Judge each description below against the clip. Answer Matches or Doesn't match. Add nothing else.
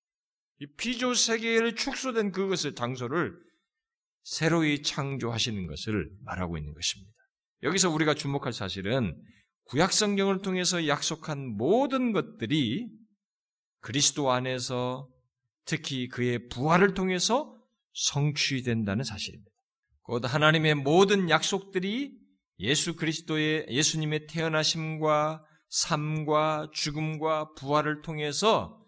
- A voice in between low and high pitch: Matches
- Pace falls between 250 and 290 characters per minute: Matches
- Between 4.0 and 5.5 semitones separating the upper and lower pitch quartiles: Doesn't match